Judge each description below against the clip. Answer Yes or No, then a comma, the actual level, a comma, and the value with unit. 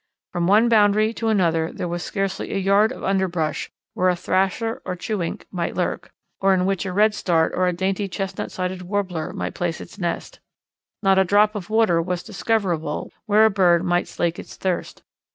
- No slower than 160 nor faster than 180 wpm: No, average, 190 wpm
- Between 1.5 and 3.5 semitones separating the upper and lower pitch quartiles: Yes, average, 2.8 semitones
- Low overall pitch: No, high, 190 Hz